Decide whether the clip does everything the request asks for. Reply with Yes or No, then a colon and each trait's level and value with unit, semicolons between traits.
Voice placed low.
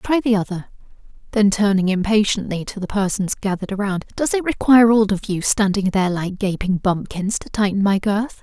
No: high, 200 Hz